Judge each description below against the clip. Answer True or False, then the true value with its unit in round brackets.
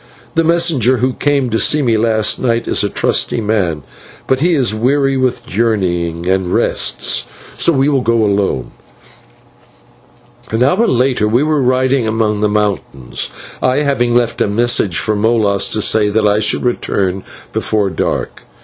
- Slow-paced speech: False (160 wpm)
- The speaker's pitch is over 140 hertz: False (115 Hz)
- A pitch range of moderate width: True (4.0 semitones)